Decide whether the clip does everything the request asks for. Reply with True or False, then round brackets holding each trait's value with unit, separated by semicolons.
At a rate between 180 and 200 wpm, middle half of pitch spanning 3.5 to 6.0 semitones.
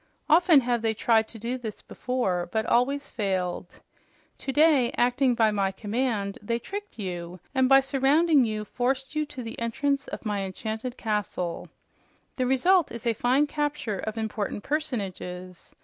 False (155 wpm; 4.5 semitones)